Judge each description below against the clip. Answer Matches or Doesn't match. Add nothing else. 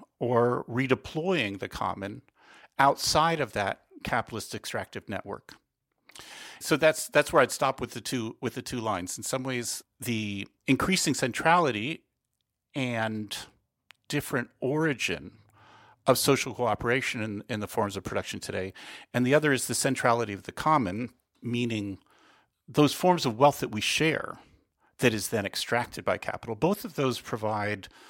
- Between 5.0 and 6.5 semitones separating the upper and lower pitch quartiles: Doesn't match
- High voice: Doesn't match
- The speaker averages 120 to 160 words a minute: Matches